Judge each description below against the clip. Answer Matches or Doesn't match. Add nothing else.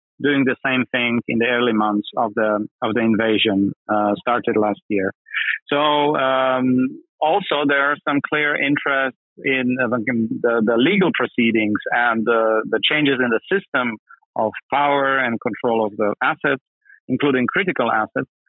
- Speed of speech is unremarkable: Doesn't match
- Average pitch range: Matches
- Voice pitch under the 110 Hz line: Doesn't match